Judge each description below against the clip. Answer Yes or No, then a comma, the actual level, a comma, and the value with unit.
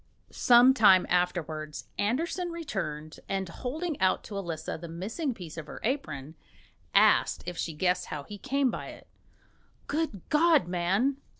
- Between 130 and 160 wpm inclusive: Yes, average, 145 wpm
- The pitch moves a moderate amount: No, wide, 8.2 semitones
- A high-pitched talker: Yes, high, 195 Hz